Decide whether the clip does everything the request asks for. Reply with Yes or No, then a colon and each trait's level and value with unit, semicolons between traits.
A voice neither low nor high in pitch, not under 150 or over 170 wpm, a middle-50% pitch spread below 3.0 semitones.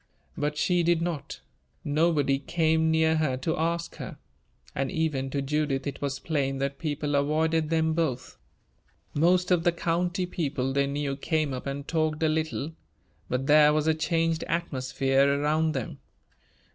Yes: medium, 155 Hz; average, 160 wpm; narrow, 2.6 semitones